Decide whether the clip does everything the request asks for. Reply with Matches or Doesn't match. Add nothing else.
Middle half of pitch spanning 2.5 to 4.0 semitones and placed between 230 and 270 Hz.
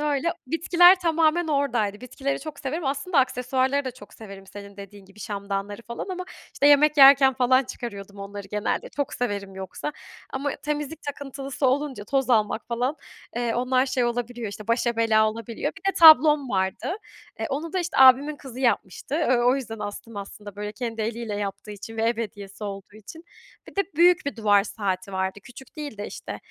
Doesn't match